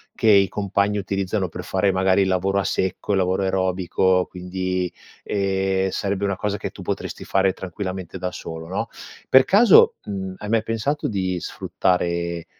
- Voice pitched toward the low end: Yes, very low, 95 Hz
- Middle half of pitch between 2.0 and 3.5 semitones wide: No, narrow, 1.4 semitones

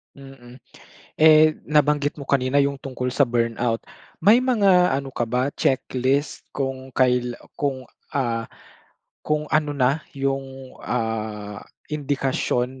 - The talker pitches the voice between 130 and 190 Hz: Yes, low, 135 Hz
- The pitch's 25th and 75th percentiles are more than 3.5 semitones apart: No, narrow, 2.6 semitones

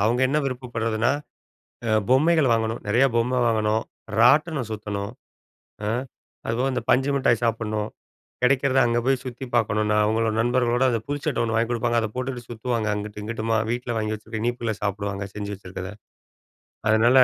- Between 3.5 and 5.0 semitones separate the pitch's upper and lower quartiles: No, narrow, 2.6 semitones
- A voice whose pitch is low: Yes, low, 115 Hz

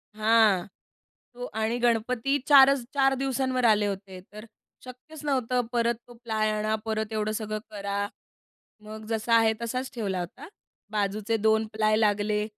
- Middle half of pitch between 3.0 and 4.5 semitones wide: No, narrow, 2.4 semitones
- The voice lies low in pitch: No, high, 220 Hz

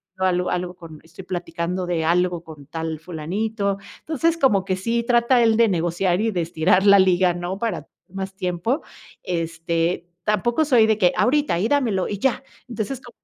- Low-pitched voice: No, medium, 185 Hz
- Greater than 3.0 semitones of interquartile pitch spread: Yes, average, 4.4 semitones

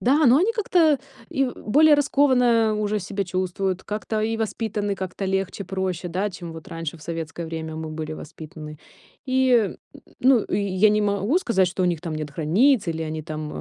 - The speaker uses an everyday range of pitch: No, wide, 6.1 semitones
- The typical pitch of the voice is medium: No, high, 195 Hz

